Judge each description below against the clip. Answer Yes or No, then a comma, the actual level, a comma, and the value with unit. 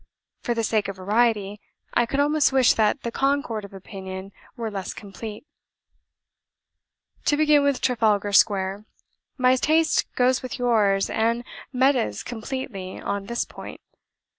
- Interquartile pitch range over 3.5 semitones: Yes, average, 4.4 semitones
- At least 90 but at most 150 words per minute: Yes, average, 140 wpm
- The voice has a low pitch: No, high, 230 Hz